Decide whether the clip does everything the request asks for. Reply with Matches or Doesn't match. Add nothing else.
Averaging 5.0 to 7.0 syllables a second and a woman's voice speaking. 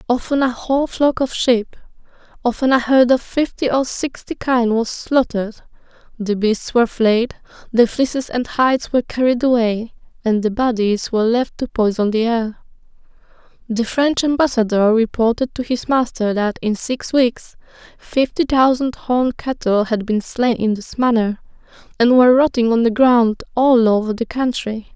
Doesn't match